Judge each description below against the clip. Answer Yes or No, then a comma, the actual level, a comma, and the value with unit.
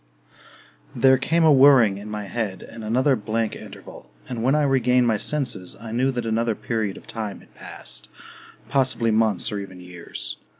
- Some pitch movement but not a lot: Yes, average, 3.6 semitones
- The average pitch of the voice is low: Yes, low, 115 Hz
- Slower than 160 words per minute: No, average, 180 wpm